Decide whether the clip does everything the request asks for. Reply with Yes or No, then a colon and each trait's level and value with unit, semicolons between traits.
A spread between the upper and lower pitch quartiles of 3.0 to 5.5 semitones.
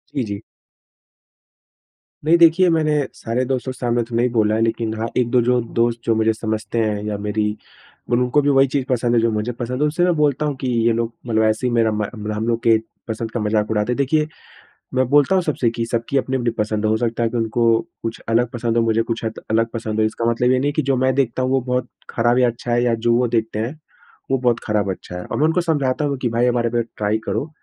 No: narrow, 2.6 semitones